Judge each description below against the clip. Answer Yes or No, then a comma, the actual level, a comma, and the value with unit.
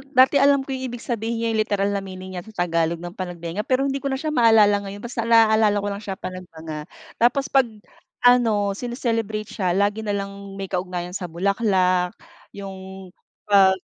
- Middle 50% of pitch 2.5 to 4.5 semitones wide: Yes, average, 3.7 semitones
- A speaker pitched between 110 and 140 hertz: No, high, 205 Hz